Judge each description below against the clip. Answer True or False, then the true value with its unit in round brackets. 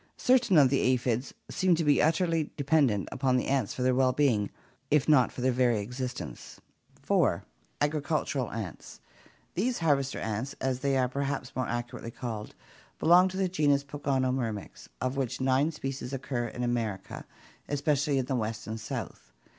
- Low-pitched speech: True (130 Hz)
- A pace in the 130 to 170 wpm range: True (160 wpm)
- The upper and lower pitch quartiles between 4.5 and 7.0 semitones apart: False (3.2 semitones)